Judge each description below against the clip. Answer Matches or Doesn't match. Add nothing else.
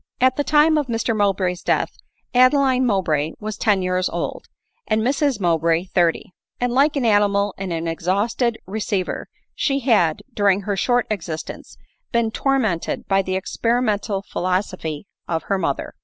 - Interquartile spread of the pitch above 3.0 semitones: Matches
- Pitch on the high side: Matches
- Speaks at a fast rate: Doesn't match